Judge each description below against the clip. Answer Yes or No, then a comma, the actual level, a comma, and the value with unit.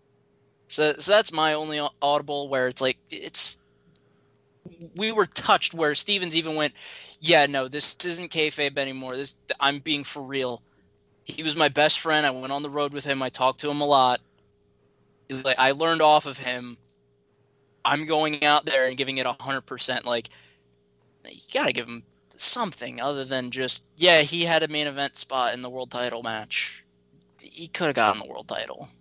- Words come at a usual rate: Yes, average, 180 wpm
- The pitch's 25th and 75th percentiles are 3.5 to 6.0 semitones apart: No, average, 3.0 semitones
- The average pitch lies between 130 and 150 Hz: Yes, medium, 140 Hz